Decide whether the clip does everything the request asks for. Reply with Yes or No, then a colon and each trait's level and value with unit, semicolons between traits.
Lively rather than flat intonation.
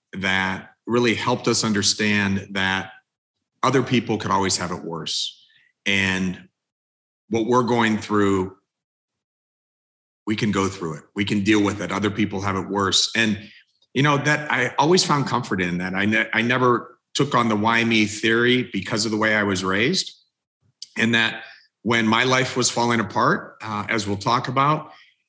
No: average, 3.4 semitones